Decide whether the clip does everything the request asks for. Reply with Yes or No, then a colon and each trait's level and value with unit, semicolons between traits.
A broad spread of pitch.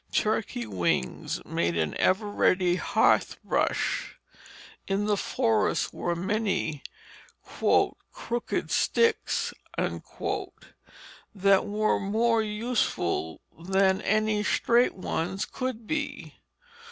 No: average, 3.7 semitones